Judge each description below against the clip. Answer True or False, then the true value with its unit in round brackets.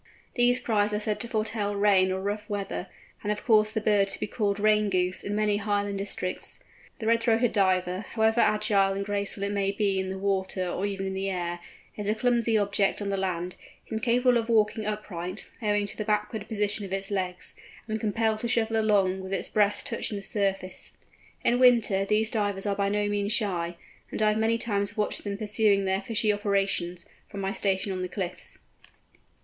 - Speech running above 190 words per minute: True (200 wpm)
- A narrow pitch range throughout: True (1.8 semitones)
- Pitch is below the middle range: False (205 Hz)